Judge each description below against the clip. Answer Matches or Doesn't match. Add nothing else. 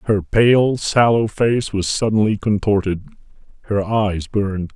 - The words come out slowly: Matches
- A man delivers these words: Matches